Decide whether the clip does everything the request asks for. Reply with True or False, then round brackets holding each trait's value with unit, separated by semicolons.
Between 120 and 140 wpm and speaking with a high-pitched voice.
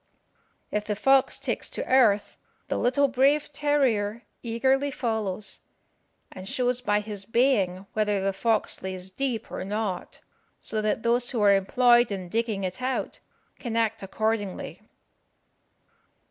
True (135 wpm; 220 Hz)